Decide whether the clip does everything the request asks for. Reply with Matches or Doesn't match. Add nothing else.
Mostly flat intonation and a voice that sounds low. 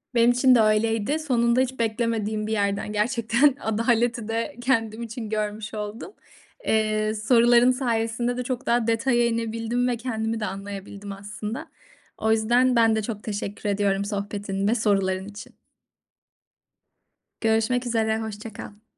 Doesn't match